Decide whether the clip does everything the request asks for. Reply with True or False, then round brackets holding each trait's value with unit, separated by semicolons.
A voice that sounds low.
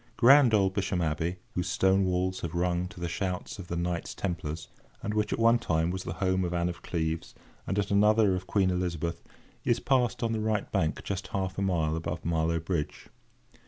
True (90 Hz)